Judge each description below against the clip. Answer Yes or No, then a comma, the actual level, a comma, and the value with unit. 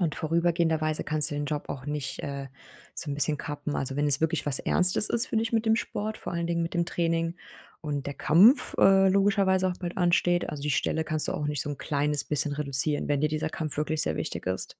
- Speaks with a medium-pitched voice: Yes, medium, 155 Hz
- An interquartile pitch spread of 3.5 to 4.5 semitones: No, average, 3.1 semitones